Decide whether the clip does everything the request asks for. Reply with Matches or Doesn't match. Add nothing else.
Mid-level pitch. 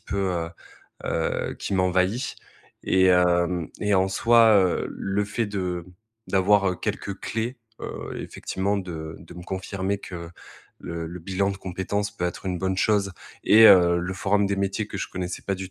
Doesn't match